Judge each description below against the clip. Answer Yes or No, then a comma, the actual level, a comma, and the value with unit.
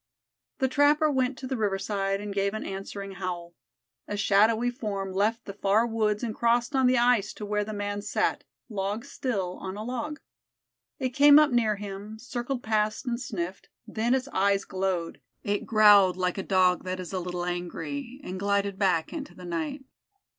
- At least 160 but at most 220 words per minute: Yes, average, 180 wpm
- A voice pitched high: Yes, high, 205 Hz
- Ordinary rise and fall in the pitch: Yes, average, 3.8 semitones